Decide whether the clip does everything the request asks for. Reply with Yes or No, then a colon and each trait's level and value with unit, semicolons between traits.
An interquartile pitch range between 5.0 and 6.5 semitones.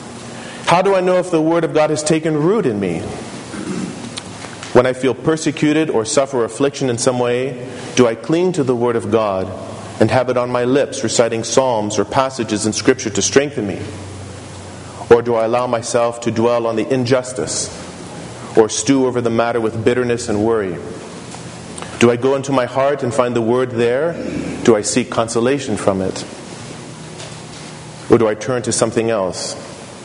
No: average, 3.1 semitones